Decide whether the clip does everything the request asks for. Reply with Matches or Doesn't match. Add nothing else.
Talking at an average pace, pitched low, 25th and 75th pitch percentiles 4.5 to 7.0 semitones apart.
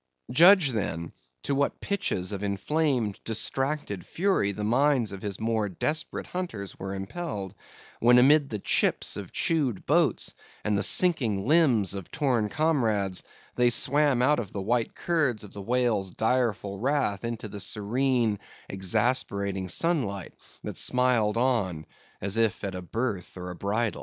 Matches